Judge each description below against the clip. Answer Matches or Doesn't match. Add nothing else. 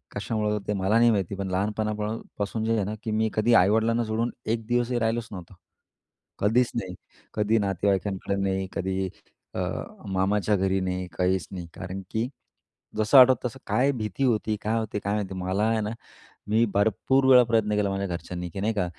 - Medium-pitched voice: Doesn't match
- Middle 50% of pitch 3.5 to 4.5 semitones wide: Doesn't match